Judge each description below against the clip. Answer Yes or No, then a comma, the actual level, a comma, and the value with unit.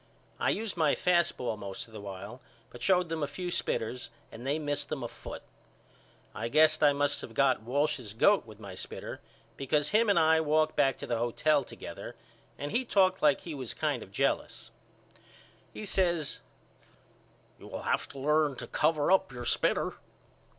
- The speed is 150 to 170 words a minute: No, average, 185 wpm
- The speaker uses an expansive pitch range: No, average, 4.9 semitones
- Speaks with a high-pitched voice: No, medium, 145 Hz